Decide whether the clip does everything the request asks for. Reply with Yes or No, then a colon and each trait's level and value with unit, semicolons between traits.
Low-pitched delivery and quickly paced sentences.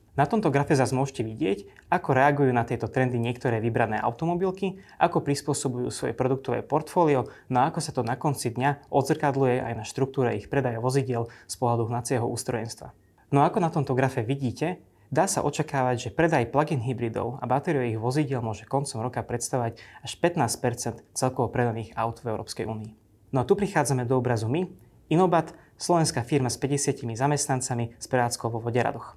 Yes: low, 130 Hz; fast, 170 wpm